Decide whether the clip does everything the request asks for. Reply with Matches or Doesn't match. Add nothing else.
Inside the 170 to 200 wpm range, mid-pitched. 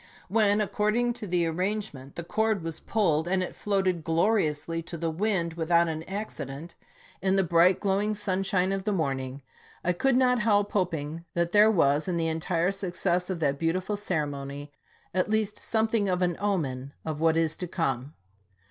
Matches